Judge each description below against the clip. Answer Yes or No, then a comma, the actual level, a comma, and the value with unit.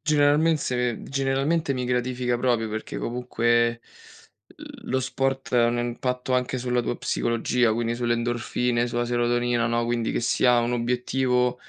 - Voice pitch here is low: Yes, low, 120 Hz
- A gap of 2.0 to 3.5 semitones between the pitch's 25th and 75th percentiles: No, narrow, 1.3 semitones